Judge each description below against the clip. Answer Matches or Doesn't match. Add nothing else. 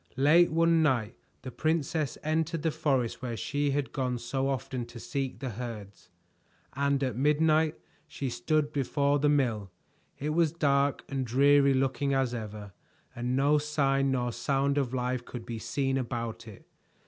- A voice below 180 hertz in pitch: Matches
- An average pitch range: Matches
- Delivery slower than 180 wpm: Matches